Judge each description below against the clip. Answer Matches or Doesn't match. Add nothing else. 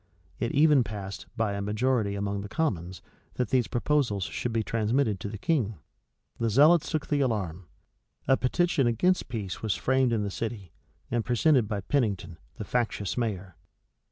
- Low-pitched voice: Matches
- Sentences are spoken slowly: Doesn't match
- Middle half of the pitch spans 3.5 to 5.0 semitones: Matches